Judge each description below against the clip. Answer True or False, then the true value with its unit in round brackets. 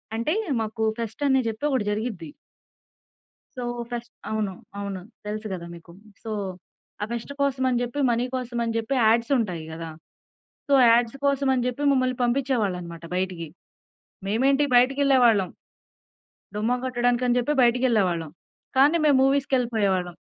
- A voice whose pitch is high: True (235 Hz)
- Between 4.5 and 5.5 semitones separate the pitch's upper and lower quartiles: False (3.8 semitones)